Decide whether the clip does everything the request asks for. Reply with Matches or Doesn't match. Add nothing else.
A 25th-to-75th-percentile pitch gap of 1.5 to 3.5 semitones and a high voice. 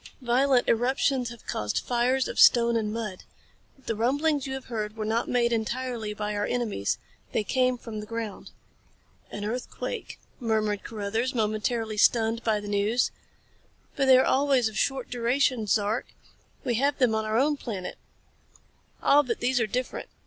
Matches